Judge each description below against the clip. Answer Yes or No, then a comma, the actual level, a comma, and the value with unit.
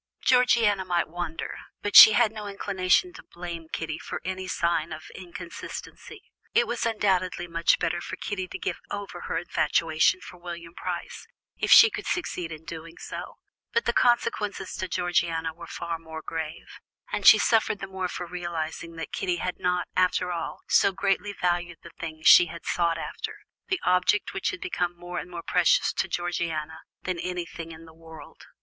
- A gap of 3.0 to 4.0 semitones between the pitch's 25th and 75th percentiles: No, narrow, 2.5 semitones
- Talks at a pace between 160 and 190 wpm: Yes, average, 180 wpm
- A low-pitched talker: No, medium, 175 Hz